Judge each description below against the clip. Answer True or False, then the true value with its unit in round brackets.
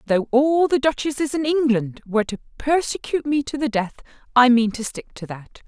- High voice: True (260 Hz)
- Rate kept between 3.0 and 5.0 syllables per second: False (5.5 syllables/s)